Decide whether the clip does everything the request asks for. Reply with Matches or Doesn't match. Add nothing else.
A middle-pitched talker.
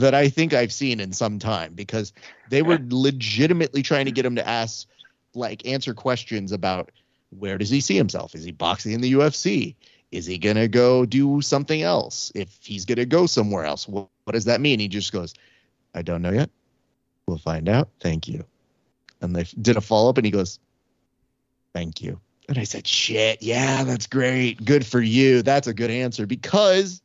Doesn't match